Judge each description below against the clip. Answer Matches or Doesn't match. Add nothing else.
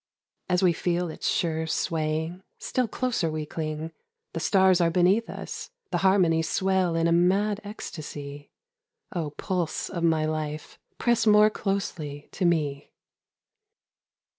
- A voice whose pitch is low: Doesn't match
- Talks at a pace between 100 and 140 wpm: Matches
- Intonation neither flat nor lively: Matches